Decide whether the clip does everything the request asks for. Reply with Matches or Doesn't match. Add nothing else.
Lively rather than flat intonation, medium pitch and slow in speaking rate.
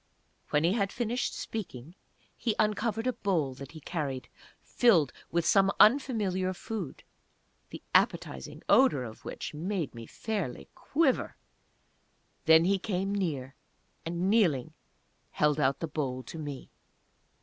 Matches